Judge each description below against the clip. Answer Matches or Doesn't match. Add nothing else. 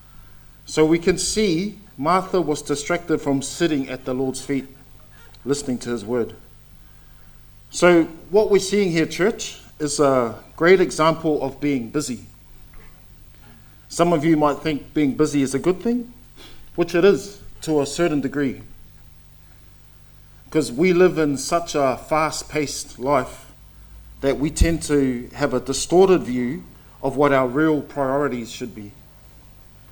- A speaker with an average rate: Matches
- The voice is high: Doesn't match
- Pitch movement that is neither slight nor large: Matches